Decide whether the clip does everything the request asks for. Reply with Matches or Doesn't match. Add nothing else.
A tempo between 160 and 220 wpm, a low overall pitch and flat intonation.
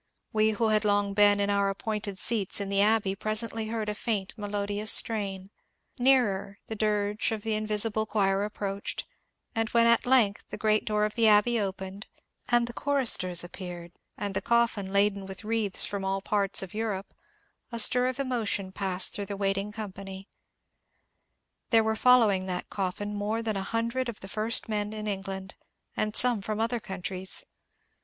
Doesn't match